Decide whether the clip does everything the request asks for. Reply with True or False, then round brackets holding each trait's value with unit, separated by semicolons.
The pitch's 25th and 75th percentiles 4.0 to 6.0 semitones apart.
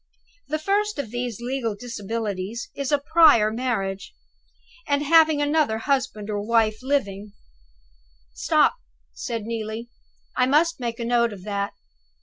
True (5.2 semitones)